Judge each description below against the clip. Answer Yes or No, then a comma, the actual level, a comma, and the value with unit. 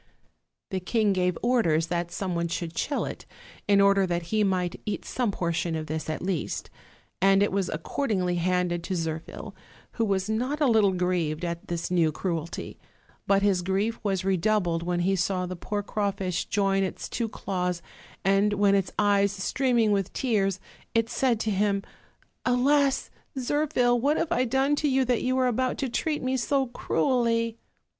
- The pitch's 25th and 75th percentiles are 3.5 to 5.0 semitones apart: Yes, average, 4.7 semitones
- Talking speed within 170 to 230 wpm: Yes, average, 180 wpm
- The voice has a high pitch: Yes, high, 200 Hz